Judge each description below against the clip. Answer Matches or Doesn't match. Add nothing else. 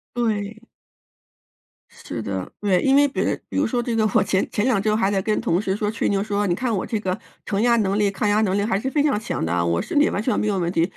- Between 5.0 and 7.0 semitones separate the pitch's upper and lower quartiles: Doesn't match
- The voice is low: Doesn't match